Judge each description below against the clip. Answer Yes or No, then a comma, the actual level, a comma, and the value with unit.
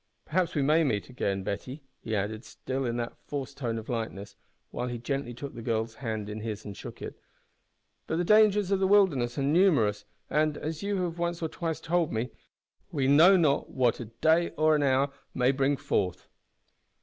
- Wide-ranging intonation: Yes, wide, 6.1 semitones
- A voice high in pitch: No, low, 135 Hz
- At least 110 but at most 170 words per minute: No, average, 195 wpm